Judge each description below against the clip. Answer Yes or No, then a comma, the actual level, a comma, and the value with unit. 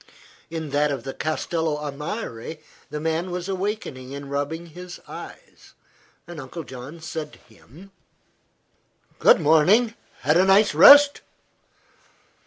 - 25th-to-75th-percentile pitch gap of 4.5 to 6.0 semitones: No, average, 3.9 semitones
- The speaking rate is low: Yes, slow, 125 wpm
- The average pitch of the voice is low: No, medium, 160 Hz